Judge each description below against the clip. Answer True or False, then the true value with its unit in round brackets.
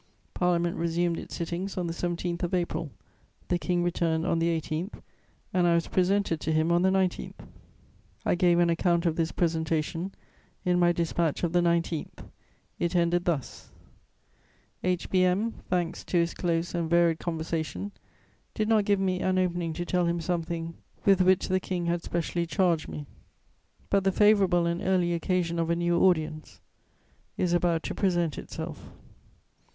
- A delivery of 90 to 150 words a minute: False (165 wpm)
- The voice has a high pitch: False (175 Hz)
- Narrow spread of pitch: True (1.3 semitones)